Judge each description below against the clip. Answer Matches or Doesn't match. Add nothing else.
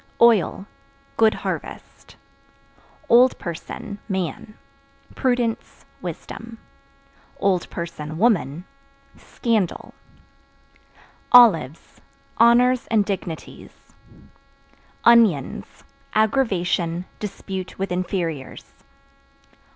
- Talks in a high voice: Matches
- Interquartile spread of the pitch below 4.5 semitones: Doesn't match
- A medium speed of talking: Doesn't match